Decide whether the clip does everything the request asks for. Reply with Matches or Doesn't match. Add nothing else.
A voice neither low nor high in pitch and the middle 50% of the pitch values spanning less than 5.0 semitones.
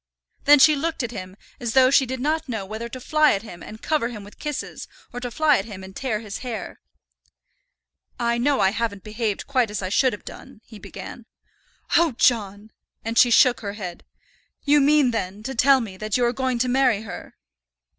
Doesn't match